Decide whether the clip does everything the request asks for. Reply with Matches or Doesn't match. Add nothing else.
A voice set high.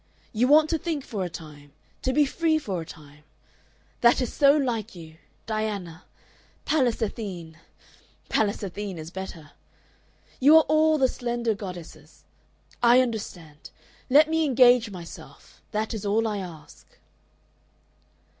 Matches